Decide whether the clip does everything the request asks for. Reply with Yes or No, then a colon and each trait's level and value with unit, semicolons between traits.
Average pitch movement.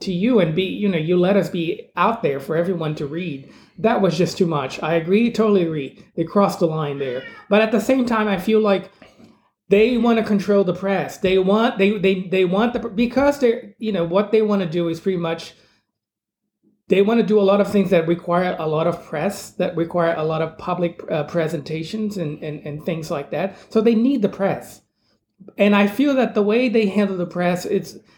Yes: average, 4.1 semitones